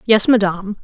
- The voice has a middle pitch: No, high, 205 Hz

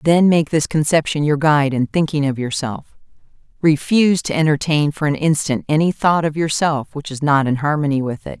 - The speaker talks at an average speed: Yes, average, 195 wpm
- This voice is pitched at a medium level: Yes, medium, 150 Hz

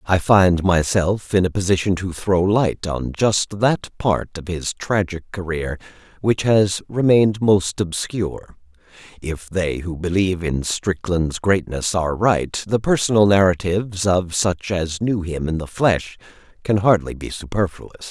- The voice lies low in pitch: Yes, very low, 95 Hz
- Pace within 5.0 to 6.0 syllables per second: No, 4.2 syllables/s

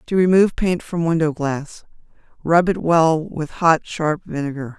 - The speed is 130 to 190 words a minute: Yes, average, 150 wpm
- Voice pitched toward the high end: No, medium, 165 Hz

